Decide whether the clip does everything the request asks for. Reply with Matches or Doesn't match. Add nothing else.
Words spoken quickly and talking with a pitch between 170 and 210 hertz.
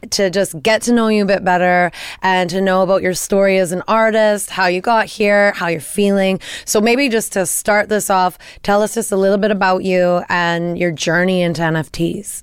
Matches